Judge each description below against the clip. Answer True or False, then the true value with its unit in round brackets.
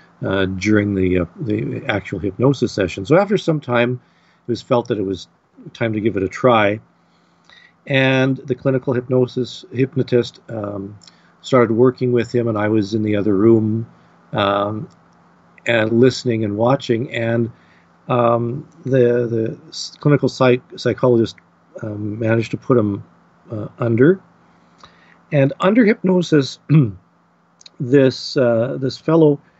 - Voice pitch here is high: False (120 Hz)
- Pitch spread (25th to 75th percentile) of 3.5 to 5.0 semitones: True (4.0 semitones)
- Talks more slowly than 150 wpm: True (135 wpm)